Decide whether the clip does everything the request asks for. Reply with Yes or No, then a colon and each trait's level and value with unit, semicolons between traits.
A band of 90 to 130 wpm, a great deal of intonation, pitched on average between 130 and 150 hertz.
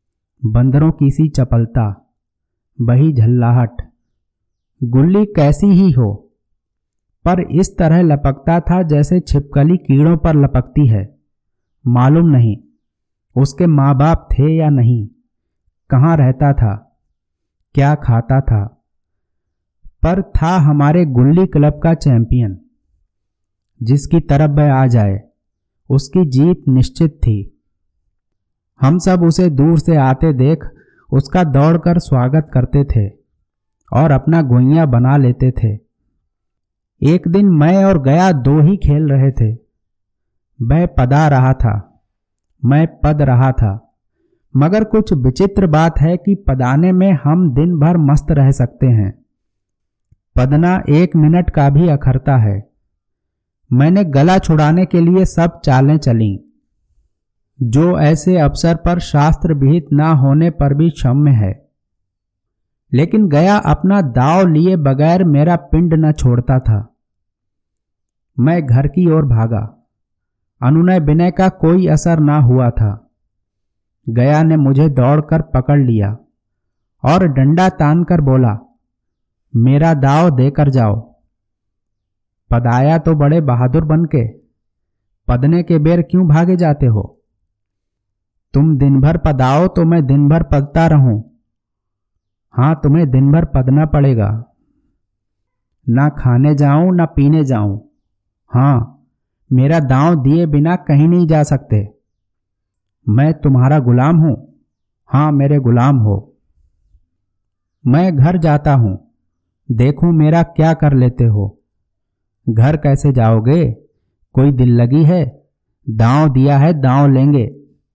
Yes: average, 125 wpm; wide, 6.4 semitones; low, 135 Hz